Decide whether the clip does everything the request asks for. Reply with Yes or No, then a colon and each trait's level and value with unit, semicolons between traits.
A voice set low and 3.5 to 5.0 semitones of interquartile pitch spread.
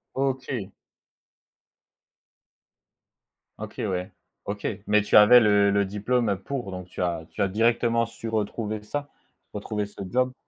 No: low, 105 Hz; average, 2.9 semitones